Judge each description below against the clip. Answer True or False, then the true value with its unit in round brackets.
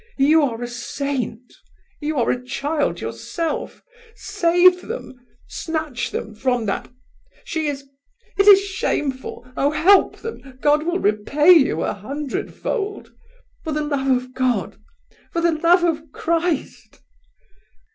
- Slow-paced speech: True (125 wpm)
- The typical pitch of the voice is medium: False (300 Hz)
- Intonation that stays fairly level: False (4.8 semitones)